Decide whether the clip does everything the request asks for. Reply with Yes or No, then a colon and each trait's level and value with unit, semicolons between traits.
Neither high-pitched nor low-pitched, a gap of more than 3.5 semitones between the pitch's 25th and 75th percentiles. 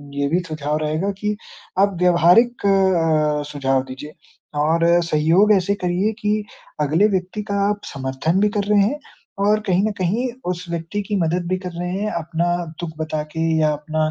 Yes: medium, 175 Hz; average, 4.5 semitones